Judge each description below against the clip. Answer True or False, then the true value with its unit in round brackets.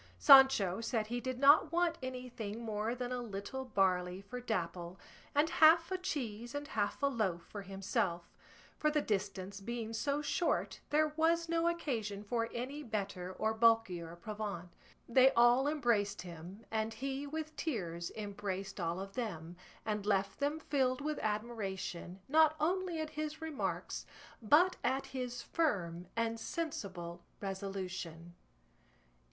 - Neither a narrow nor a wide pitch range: False (6.5 semitones)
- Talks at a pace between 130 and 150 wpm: True (145 wpm)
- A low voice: False (225 Hz)